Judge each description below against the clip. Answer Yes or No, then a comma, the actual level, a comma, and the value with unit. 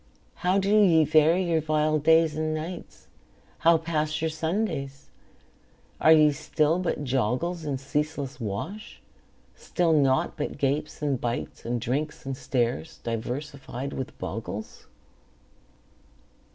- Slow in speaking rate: Yes, slow, 125 wpm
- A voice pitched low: No, medium, 150 Hz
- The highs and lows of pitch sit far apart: No, average, 3.2 semitones